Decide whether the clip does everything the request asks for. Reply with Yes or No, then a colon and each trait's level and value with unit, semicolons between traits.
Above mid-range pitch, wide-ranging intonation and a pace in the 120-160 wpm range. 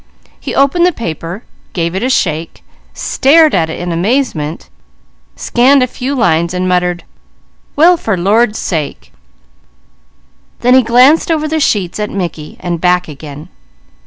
Yes: high, 195 Hz; wide, 7.5 semitones; average, 150 wpm